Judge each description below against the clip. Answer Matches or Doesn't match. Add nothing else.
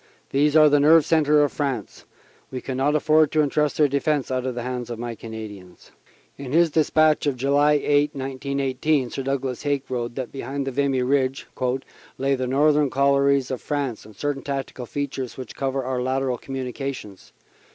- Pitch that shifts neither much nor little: Doesn't match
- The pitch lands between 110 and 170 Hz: Matches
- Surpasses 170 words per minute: Matches